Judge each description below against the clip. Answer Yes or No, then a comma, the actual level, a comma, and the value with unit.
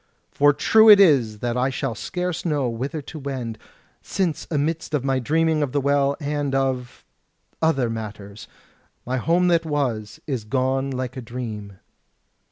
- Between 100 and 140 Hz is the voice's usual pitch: Yes, low, 135 Hz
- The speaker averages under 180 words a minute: Yes, average, 155 wpm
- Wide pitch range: No, average, 3.8 semitones